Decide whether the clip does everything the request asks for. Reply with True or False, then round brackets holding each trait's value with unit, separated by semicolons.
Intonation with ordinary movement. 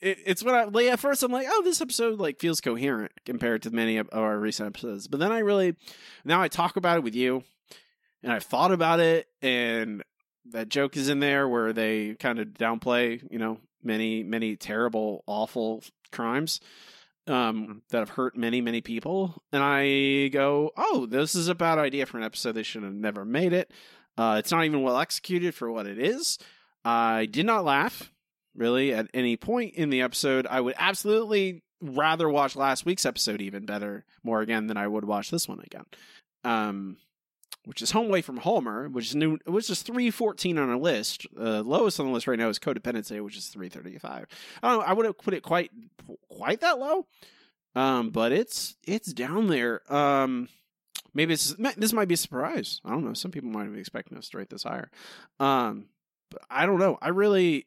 False (7.9 semitones)